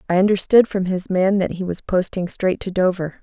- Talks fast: Yes, fast, 225 wpm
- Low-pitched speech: No, medium, 185 Hz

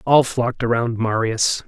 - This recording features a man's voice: Yes, male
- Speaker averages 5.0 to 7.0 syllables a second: No, 4.6 syllables/s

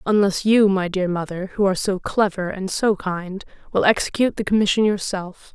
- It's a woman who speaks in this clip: Yes, female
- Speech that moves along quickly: No, average, 185 wpm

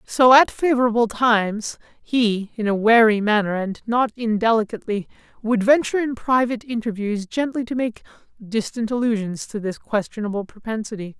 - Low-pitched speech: No, high, 225 Hz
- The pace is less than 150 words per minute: Yes, average, 140 wpm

